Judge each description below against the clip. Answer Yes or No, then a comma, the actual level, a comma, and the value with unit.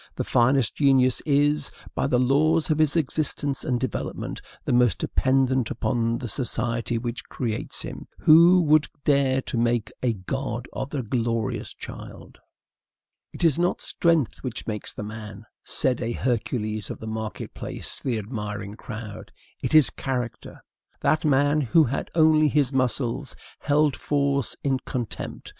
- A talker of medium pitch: No, low, 130 Hz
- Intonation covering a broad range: No, average, 3.8 semitones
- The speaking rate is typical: Yes, average, 150 wpm